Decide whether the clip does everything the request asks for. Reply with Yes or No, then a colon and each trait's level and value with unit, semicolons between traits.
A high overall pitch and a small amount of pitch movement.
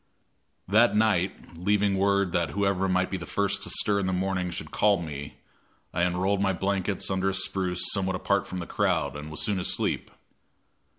No: very low, 95 Hz; narrow, 1.8 semitones